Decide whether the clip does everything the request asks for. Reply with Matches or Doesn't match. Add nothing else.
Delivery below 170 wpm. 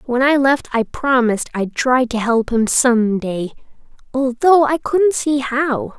Matches